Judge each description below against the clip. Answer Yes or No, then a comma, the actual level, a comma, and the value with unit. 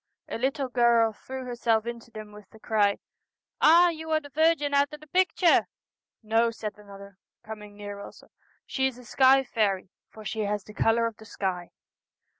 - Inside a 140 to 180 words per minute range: No, fast, 205 wpm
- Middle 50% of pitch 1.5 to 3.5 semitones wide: No, average, 4.3 semitones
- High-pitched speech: Yes, high, 230 Hz